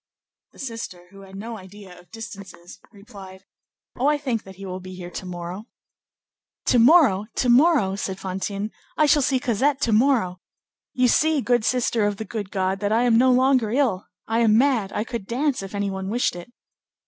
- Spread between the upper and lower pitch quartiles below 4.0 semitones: No, average, 4.6 semitones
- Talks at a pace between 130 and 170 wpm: No, average, 195 wpm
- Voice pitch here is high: Yes, high, 215 Hz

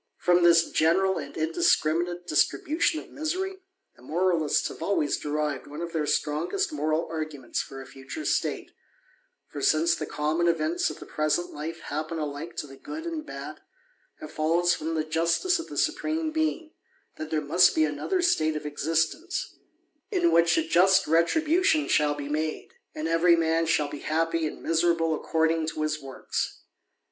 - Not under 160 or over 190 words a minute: Yes, average, 175 wpm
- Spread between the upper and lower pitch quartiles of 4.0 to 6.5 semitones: No, average, 3.6 semitones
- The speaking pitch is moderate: Yes, medium, 165 Hz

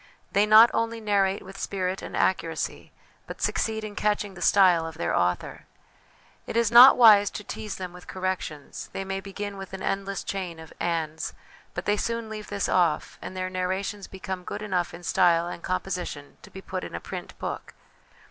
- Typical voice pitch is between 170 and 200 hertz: Yes, high, 190 Hz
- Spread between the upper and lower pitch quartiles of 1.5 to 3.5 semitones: Yes, narrow, 2.6 semitones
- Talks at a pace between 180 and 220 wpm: Yes, average, 195 wpm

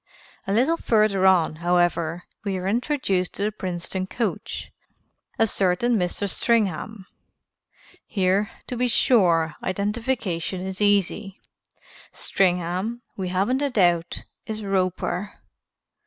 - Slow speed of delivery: Yes, slow, 110 wpm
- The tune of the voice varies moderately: Yes, average, 3.4 semitones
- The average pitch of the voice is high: Yes, high, 195 Hz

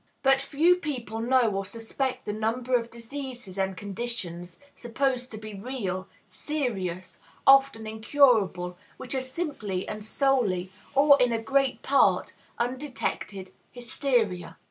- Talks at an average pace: No, slow, 125 wpm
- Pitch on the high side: Yes, high, 235 Hz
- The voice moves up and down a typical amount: Yes, average, 5.0 semitones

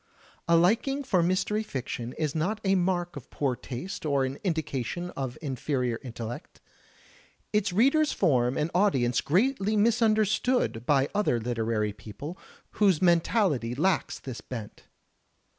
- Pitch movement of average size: No, wide, 8.0 semitones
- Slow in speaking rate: Yes, slow, 130 wpm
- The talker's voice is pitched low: No, medium, 160 Hz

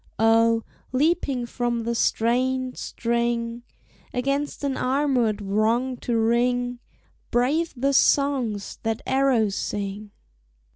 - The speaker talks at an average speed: No, slow, 100 wpm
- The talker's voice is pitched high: Yes, high, 240 Hz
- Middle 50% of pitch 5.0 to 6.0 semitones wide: No, narrow, 2.5 semitones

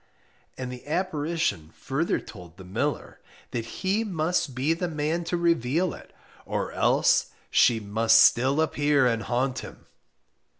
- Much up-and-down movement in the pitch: Yes, wide, 5.9 semitones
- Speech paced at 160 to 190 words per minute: No, average, 140 wpm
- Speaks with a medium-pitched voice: Yes, medium, 145 Hz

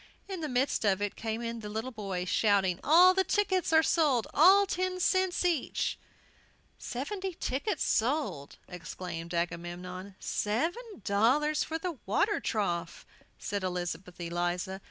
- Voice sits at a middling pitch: No, high, 230 Hz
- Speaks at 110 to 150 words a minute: Yes, slow, 135 wpm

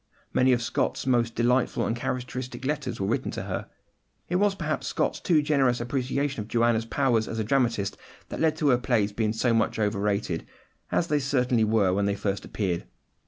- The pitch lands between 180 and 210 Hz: No, low, 120 Hz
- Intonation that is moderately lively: Yes, average, 3.7 semitones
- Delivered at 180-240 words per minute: Yes, average, 190 wpm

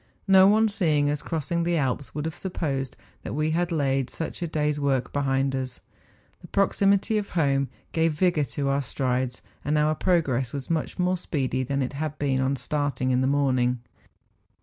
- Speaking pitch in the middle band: Yes, medium, 145 Hz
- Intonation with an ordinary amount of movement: Yes, average, 3.8 semitones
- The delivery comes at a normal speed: Yes, average, 185 wpm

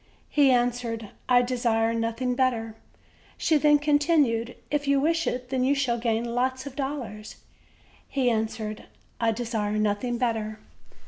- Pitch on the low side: No, high, 245 Hz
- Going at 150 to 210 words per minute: No, average, 140 wpm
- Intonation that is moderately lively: Yes, average, 3.1 semitones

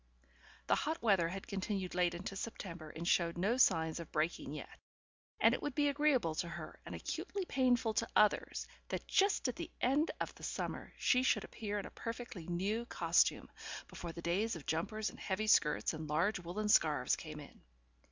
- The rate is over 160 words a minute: Yes, average, 190 wpm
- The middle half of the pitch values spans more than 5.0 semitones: Yes, wide, 5.5 semitones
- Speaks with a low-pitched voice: No, high, 195 Hz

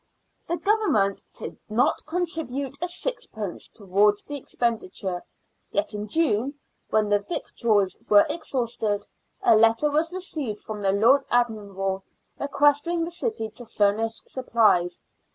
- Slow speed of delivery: Yes, slow, 125 wpm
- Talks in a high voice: Yes, high, 230 Hz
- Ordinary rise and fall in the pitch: No, wide, 6.4 semitones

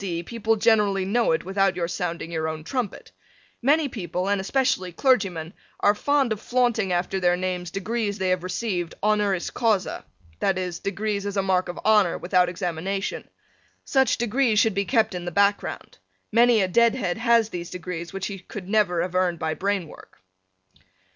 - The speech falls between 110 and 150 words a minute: No, average, 175 wpm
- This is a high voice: Yes, high, 195 Hz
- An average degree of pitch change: Yes, average, 3.5 semitones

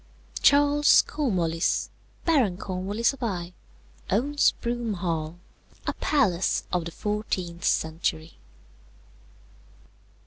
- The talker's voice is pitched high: Yes, high, 195 Hz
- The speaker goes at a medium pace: No, slow, 90 wpm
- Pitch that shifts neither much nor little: No, wide, 6.2 semitones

